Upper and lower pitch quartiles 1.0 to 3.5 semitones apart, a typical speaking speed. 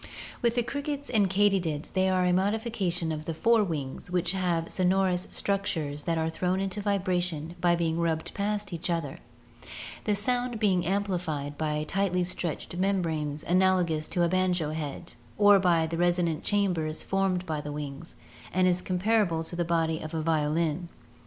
Yes: average, 3.2 semitones; average, 160 wpm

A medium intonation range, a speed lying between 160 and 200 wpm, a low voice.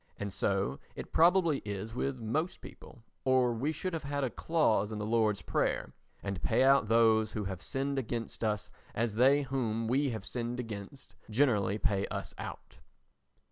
Yes: average, 4.4 semitones; average, 175 wpm; low, 115 Hz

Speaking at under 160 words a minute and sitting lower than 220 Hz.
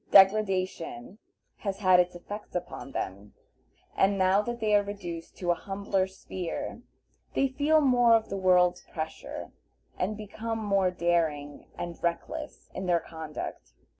Yes: average, 140 wpm; high, 190 Hz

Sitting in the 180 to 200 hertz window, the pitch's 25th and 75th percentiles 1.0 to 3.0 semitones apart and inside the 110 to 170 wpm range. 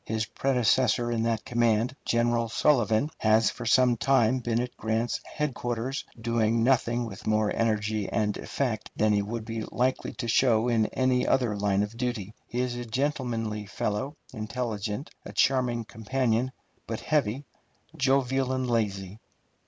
No: low, 115 Hz; narrow, 2.6 semitones; average, 150 wpm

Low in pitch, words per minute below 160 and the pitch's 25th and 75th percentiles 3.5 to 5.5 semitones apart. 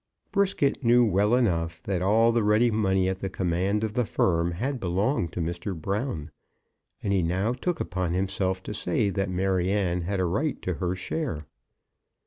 No: very low, 95 Hz; average, 175 wpm; average, 3.8 semitones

